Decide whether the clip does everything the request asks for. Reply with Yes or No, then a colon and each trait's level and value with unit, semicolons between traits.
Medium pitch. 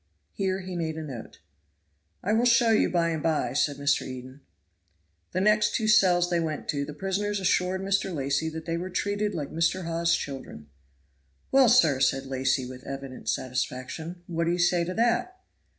Yes: medium, 170 Hz